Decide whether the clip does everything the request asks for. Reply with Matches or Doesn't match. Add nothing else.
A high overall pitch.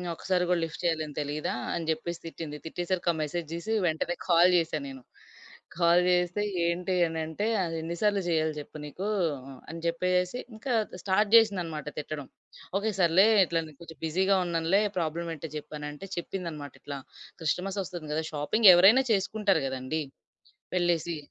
Doesn't match